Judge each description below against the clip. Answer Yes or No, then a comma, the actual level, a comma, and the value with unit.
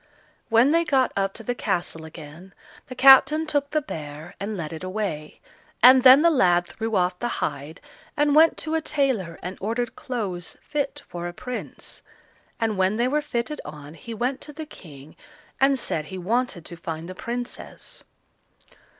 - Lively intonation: Yes, wide, 7.5 semitones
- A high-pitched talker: Yes, high, 225 Hz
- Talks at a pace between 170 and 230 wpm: Yes, average, 175 wpm